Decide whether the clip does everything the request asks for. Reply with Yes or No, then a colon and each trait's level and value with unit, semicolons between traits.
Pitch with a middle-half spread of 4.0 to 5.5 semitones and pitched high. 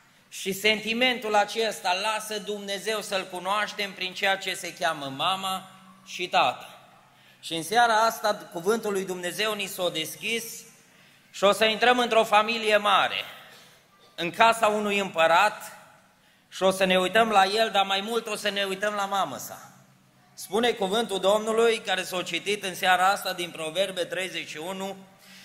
No: narrow, 2.6 semitones; high, 195 Hz